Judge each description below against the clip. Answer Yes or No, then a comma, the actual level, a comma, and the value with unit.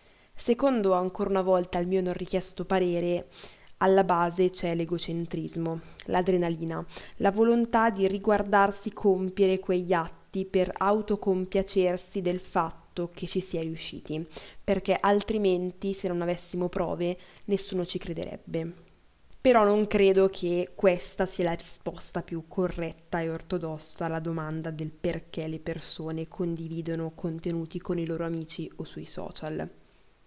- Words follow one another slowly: No, average, 130 wpm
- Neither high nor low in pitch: Yes, medium, 180 Hz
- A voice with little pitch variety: Yes, narrow, 2.3 semitones